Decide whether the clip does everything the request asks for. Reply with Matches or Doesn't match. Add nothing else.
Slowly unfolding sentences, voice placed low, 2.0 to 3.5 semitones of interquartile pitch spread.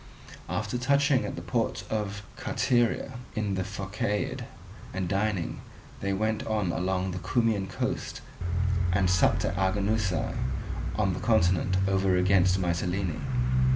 Matches